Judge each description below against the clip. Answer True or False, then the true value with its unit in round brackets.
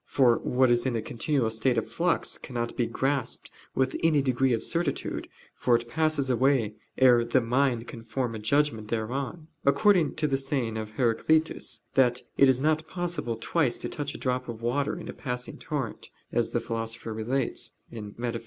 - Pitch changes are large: False (3.3 semitones)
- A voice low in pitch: True (125 Hz)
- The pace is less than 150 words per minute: False (180 wpm)